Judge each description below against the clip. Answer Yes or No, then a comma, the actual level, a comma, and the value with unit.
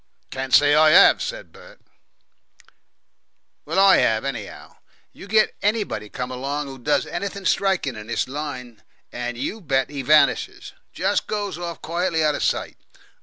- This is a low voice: No, medium, 150 Hz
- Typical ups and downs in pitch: No, wide, 6.5 semitones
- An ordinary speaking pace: Yes, average, 155 wpm